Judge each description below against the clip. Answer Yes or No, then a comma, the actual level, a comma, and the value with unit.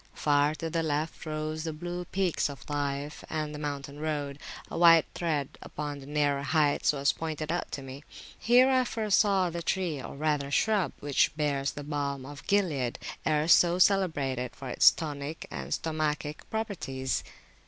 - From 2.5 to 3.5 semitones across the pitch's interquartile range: Yes, average, 2.9 semitones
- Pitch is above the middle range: No, medium, 150 Hz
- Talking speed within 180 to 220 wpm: No, average, 170 wpm